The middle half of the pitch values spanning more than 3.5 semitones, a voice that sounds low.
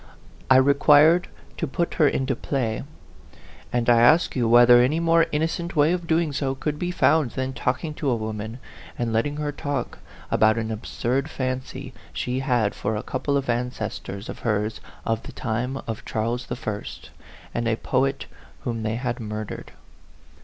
Yes: average, 4.1 semitones; low, 130 Hz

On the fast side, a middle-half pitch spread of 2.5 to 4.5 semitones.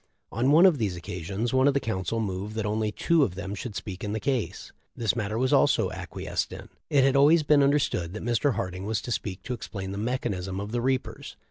No: fast, 230 wpm; average, 5.0 semitones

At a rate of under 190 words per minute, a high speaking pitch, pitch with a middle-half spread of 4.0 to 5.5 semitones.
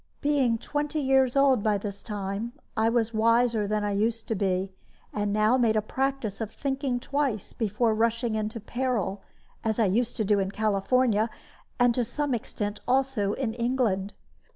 No: average, 170 wpm; high, 225 Hz; average, 3.3 semitones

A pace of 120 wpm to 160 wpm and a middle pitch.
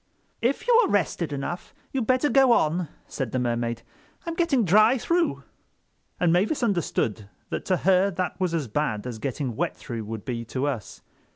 No: average, 180 wpm; medium, 170 Hz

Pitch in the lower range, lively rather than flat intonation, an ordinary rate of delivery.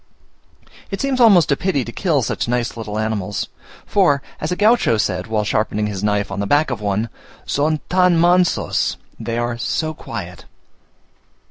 Yes: low, 120 Hz; wide, 8.4 semitones; average, 165 wpm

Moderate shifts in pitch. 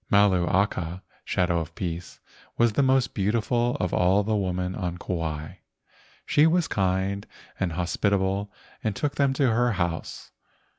Yes: average, 4.0 semitones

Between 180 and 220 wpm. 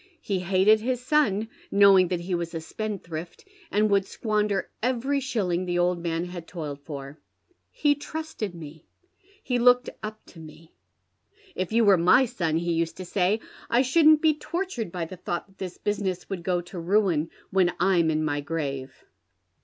Yes: average, 185 wpm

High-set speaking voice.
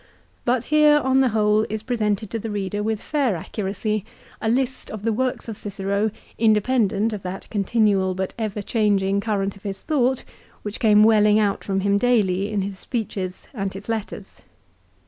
Yes: high, 210 Hz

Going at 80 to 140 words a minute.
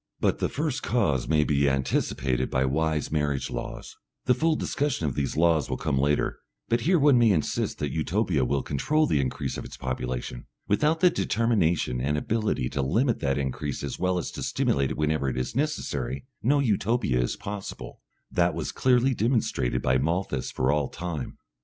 No: average, 185 wpm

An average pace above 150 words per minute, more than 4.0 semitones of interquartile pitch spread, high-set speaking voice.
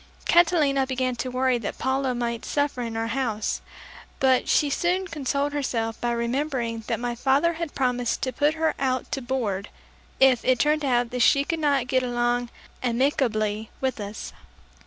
No: average, 170 wpm; average, 3.0 semitones; very high, 255 Hz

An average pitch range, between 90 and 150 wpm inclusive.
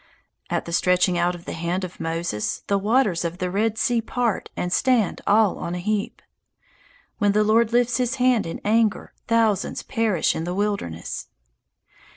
No: average, 4.3 semitones; average, 175 wpm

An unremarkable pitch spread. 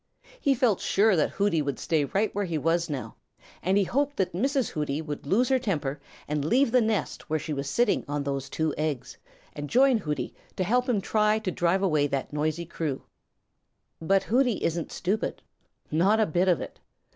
No: wide, 6.4 semitones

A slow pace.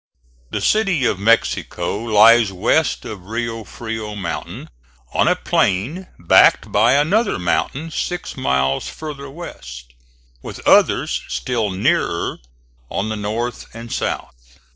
Yes: slow, 120 wpm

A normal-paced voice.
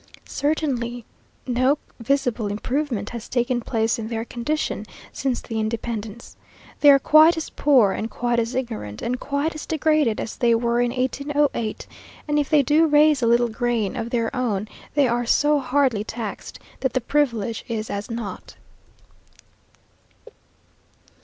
Yes: average, 150 wpm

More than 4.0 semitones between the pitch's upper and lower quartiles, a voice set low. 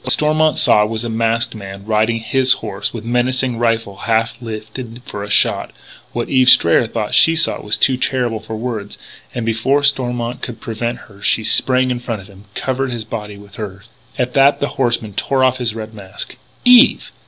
No: average, 2.9 semitones; low, 115 Hz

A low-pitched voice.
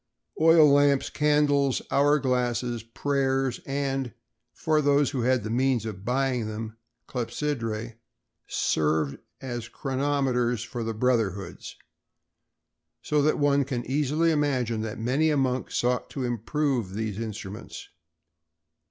Yes: low, 125 Hz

